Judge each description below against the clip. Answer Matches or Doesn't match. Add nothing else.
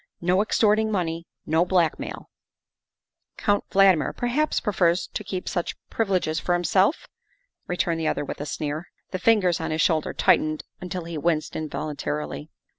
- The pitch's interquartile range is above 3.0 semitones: Matches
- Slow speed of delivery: Doesn't match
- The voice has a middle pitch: Matches